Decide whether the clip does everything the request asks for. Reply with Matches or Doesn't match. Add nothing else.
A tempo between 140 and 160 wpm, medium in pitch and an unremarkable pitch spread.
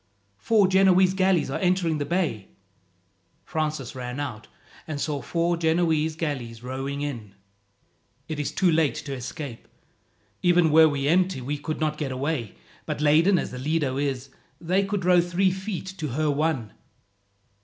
Matches